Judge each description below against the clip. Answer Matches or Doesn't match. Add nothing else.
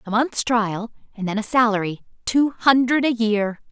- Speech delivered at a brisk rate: Doesn't match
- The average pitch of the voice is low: Doesn't match